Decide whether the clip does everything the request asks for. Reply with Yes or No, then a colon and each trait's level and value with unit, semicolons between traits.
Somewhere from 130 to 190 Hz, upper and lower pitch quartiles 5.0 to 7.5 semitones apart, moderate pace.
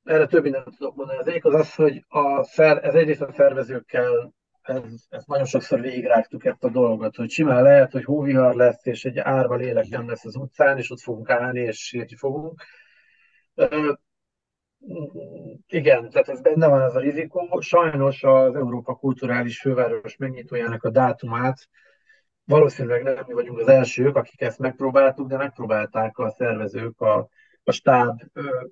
No: low, 135 Hz; wide, 5.4 semitones; fast, 160 wpm